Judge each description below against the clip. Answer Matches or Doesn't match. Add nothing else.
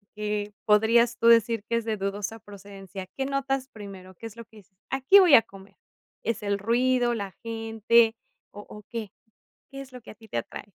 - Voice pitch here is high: Matches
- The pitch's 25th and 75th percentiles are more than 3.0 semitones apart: Doesn't match